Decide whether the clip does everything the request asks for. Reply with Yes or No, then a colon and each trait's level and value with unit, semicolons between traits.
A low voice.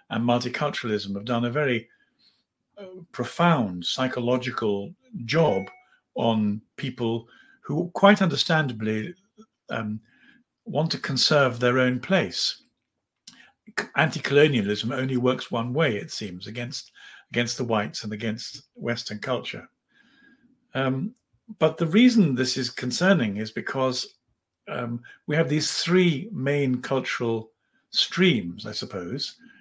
Yes: low, 130 Hz